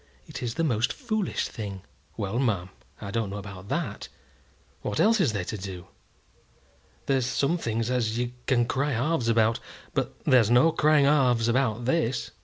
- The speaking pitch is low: Yes, low, 120 Hz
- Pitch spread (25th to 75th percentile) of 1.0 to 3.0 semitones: No, average, 4.2 semitones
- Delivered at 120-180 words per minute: Yes, average, 170 wpm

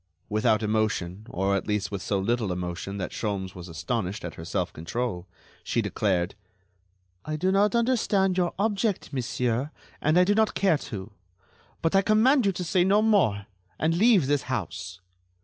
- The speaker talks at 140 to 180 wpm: Yes, average, 170 wpm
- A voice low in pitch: Yes, low, 120 Hz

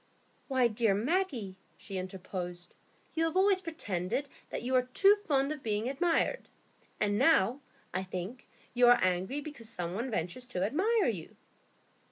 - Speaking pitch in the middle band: No, high, 245 Hz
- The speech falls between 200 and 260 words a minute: No, average, 155 wpm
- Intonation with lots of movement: Yes, wide, 7.7 semitones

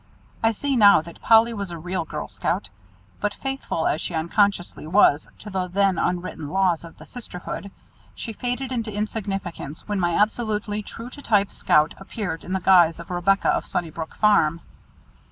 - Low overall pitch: No, high, 195 Hz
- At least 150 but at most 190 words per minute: Yes, average, 170 wpm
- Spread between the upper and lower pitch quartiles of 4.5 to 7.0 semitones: No, average, 4.0 semitones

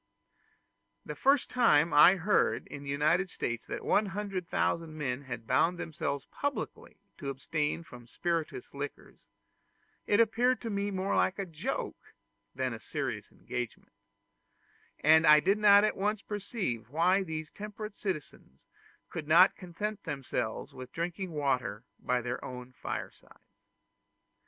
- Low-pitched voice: No, medium, 165 Hz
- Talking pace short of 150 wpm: Yes, slow, 135 wpm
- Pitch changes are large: Yes, wide, 6.4 semitones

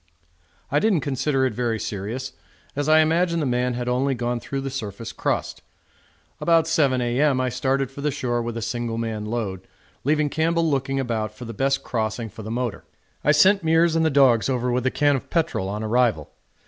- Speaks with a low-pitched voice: Yes, low, 130 Hz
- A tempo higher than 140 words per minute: Yes, average, 200 wpm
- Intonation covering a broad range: No, average, 4.0 semitones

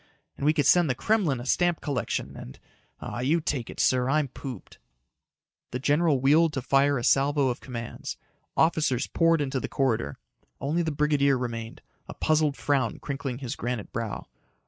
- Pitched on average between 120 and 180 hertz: Yes, medium, 140 Hz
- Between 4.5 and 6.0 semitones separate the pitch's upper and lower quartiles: No, average, 3.4 semitones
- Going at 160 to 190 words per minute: Yes, average, 170 wpm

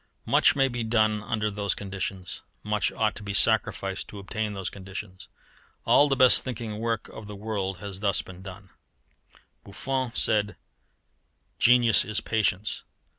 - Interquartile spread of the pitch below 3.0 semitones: Yes, narrow, 2.6 semitones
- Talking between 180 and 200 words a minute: No, average, 150 wpm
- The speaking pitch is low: Yes, low, 105 Hz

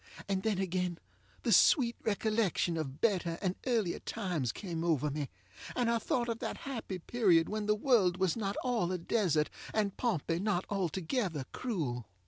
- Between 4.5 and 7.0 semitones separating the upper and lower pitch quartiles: Yes, average, 4.8 semitones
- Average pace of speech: Yes, average, 165 wpm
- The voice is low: No, high, 190 Hz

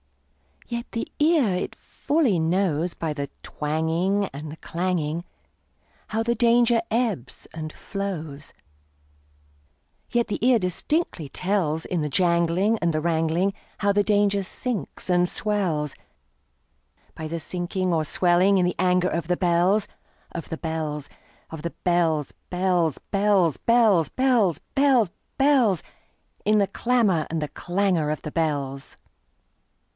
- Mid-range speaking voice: Yes, medium, 175 Hz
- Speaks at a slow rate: Yes, slow, 110 wpm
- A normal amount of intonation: Yes, average, 4.6 semitones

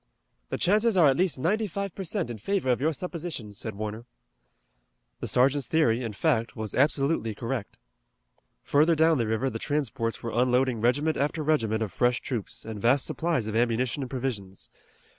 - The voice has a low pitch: Yes, low, 130 Hz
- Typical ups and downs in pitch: No, wide, 5.8 semitones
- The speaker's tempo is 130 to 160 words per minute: No, average, 180 wpm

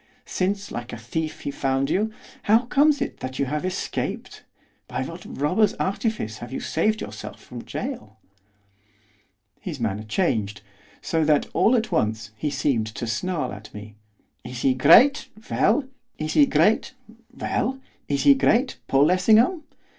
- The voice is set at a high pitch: No, medium, 155 Hz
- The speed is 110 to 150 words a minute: Yes, average, 140 wpm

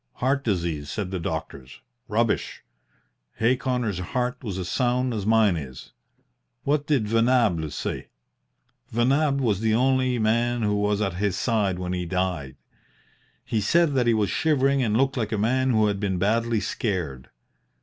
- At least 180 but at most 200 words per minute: No, average, 160 wpm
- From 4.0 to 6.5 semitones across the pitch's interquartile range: Yes, average, 4.8 semitones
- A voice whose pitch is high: No, low, 110 Hz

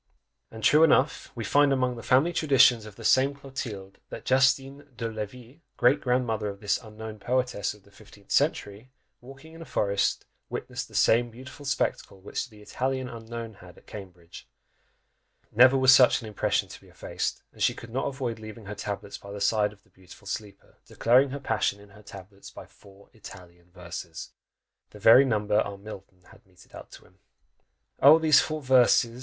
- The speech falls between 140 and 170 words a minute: No, average, 185 wpm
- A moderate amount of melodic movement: Yes, average, 4.5 semitones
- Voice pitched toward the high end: No, low, 115 Hz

